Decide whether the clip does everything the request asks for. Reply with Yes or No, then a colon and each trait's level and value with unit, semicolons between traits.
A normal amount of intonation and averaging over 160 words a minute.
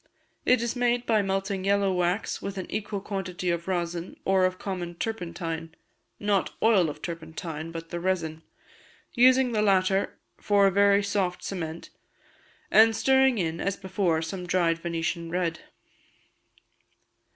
No: average, 3.1 semitones; average, 140 wpm